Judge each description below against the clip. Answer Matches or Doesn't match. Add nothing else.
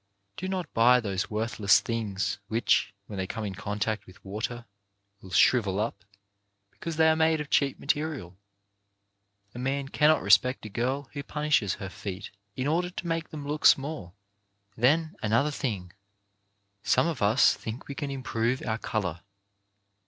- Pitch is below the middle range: Matches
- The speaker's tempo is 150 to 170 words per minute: Matches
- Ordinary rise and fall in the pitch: Doesn't match